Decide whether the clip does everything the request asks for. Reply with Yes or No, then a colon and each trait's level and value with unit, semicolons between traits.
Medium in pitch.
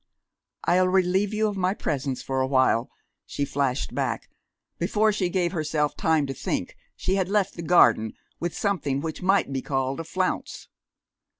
Yes: medium, 170 Hz